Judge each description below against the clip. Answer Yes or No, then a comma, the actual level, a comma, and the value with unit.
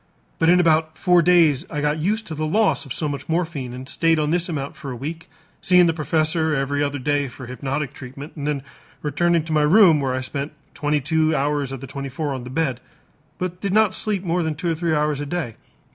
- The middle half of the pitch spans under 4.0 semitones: Yes, average, 3.2 semitones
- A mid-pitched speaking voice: Yes, medium, 150 Hz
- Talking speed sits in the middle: No, fast, 235 wpm